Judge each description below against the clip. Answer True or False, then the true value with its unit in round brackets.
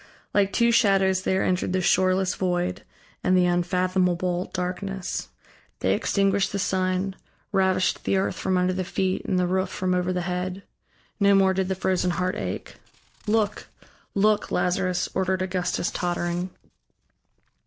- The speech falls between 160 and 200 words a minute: False (145 wpm)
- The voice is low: False (185 Hz)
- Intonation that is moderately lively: False (1.0 semitones)